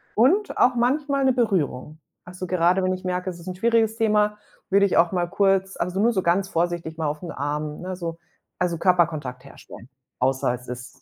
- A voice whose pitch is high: No, medium, 180 Hz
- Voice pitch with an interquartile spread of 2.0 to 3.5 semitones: No, average, 4.1 semitones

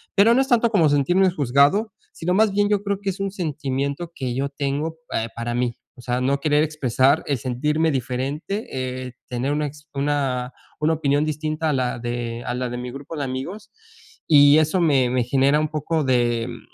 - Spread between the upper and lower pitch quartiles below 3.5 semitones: No, average, 4.0 semitones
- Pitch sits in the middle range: Yes, medium, 145 Hz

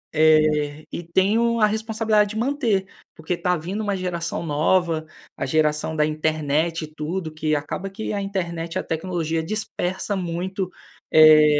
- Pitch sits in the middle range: Yes, medium, 170 Hz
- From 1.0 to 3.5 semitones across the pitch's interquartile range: No, average, 4.0 semitones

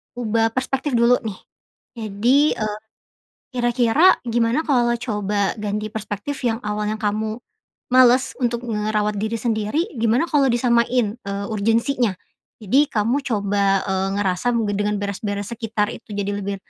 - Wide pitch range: No, average, 2.9 semitones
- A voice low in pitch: No, high, 225 Hz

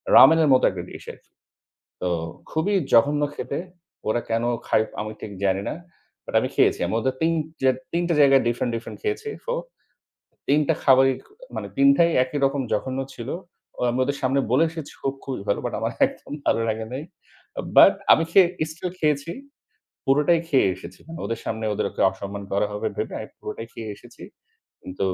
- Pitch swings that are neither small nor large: No, wide, 6.0 semitones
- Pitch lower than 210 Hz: Yes, low, 135 Hz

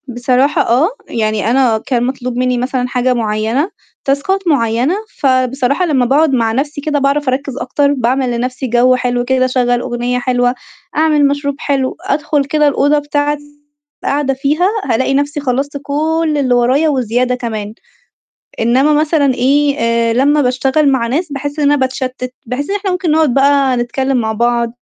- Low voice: No, very high, 265 Hz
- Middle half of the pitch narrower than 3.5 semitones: Yes, average, 2.8 semitones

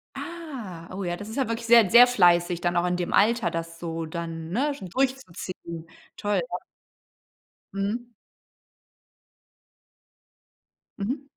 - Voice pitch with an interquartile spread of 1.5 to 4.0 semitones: No, wide, 5.5 semitones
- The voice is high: Yes, high, 195 Hz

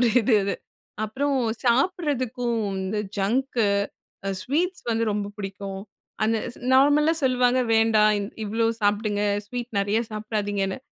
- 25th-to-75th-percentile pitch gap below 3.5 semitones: No, average, 4.0 semitones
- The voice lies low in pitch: No, high, 225 Hz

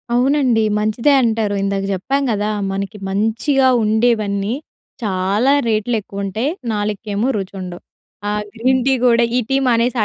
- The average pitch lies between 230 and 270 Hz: No, high, 220 Hz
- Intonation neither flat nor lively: Yes, average, 3.4 semitones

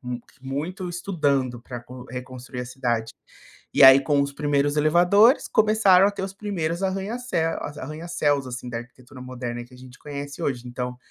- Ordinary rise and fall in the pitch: No, wide, 5.7 semitones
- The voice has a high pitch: No, medium, 140 Hz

